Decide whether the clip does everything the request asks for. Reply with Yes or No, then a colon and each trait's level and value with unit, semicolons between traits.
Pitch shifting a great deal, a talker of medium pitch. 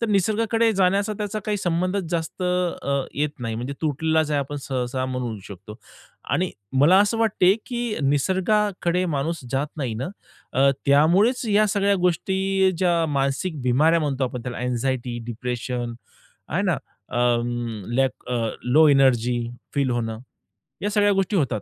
Yes: wide, 7.0 semitones; medium, 155 Hz